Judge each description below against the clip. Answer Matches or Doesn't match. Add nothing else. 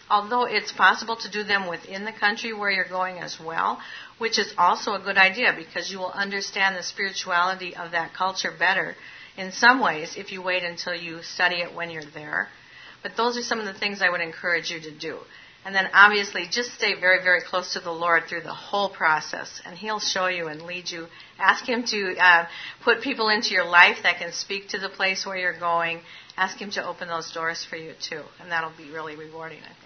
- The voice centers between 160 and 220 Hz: Matches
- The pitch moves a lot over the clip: Doesn't match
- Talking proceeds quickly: Matches